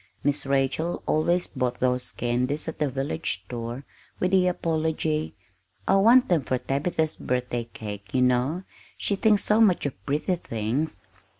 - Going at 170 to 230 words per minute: No, average, 155 wpm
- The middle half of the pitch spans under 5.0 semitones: No, average, 5.3 semitones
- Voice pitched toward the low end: No, medium, 145 Hz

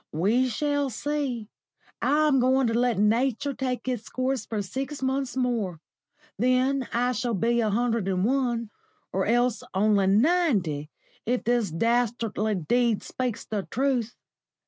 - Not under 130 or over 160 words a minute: Yes, average, 140 wpm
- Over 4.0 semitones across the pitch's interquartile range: No, average, 3.4 semitones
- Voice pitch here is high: Yes, high, 240 Hz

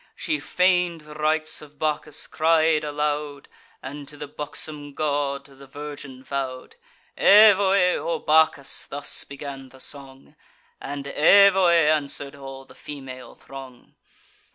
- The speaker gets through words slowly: Yes, slow, 125 wpm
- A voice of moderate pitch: Yes, medium, 145 Hz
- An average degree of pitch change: No, narrow, 2.2 semitones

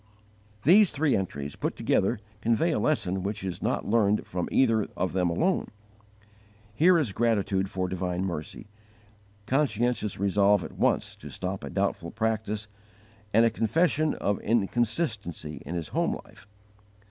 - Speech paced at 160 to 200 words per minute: No, average, 145 wpm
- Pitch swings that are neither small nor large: Yes, average, 4.2 semitones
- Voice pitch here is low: Yes, low, 105 Hz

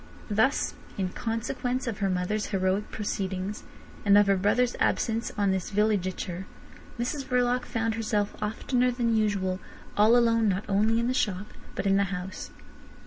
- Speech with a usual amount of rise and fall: Yes, average, 3.1 semitones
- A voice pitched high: Yes, high, 210 Hz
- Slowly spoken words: No, average, 155 wpm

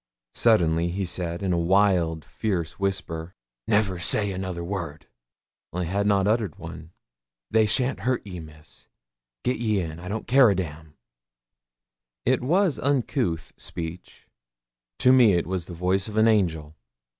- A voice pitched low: Yes, very low, 95 Hz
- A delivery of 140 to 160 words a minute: Yes, average, 155 wpm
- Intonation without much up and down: No, average, 4.3 semitones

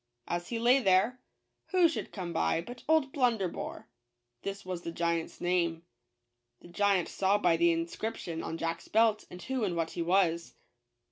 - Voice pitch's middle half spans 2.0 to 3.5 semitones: No, average, 5.1 semitones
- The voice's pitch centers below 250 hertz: Yes, medium, 185 Hz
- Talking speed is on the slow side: No, average, 160 wpm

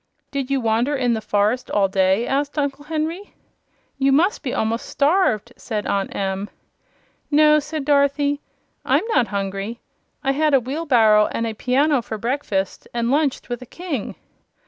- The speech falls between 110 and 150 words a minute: No, average, 160 wpm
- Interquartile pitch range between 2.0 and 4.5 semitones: No, average, 4.9 semitones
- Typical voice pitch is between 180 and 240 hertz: No, very high, 255 Hz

